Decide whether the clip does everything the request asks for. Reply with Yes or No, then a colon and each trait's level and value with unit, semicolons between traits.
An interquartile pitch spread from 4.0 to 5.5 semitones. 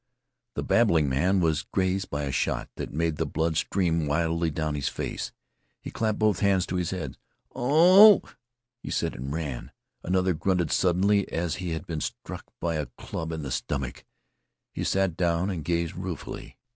No: average, 3.5 semitones